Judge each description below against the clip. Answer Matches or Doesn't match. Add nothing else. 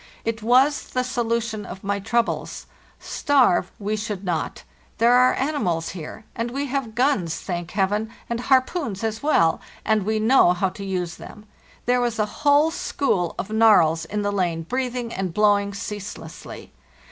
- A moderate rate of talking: Matches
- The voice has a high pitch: Matches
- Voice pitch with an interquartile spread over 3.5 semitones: Matches